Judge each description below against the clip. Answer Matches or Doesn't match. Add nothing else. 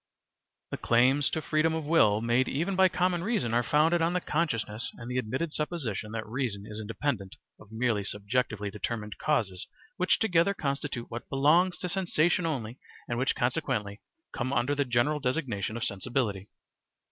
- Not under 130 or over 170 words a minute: Matches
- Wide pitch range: Matches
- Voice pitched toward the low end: Matches